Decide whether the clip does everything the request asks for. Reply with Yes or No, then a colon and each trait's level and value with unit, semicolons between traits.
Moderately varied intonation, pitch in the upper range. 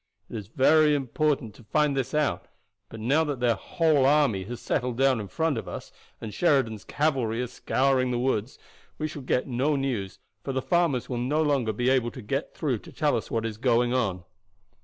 No: average, 4.0 semitones; low, 130 Hz